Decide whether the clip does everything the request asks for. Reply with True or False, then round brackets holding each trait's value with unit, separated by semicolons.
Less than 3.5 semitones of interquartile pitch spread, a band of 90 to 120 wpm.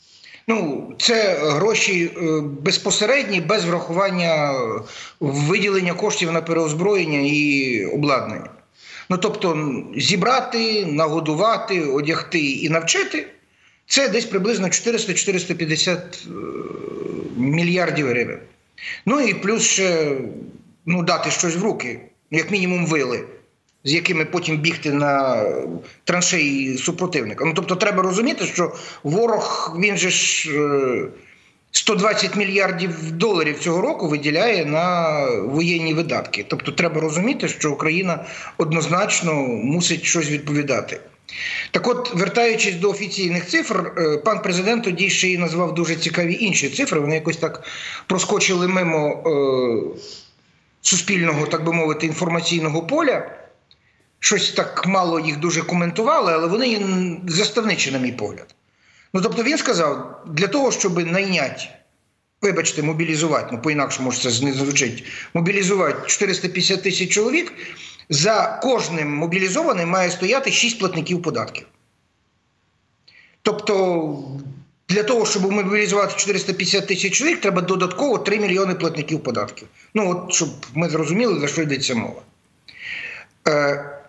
False (4.1 semitones; 115 wpm)